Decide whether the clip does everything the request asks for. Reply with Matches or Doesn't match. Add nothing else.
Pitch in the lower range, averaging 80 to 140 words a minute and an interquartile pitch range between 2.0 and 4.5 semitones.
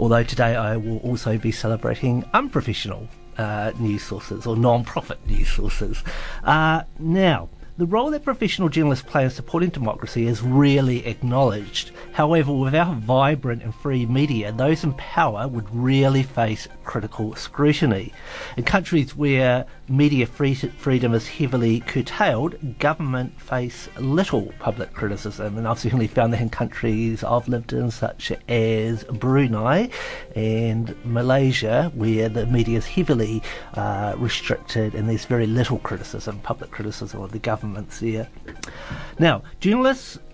Matches